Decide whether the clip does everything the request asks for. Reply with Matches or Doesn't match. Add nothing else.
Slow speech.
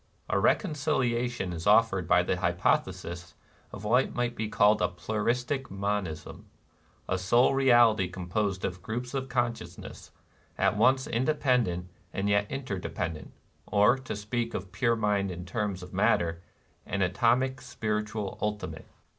Doesn't match